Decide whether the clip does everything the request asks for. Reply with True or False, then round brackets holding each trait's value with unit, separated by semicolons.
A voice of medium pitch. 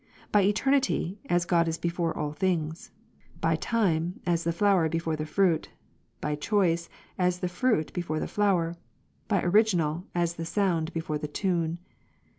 True (170 Hz)